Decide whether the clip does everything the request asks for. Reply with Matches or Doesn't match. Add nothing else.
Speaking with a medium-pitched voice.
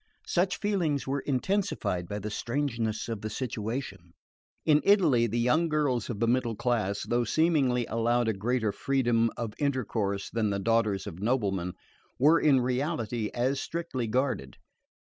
Doesn't match